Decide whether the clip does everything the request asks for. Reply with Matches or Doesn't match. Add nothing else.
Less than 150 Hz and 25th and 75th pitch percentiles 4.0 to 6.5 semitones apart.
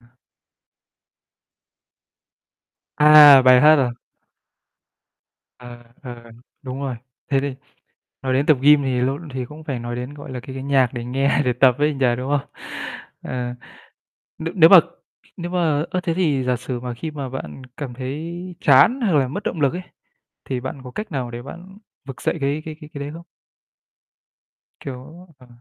Doesn't match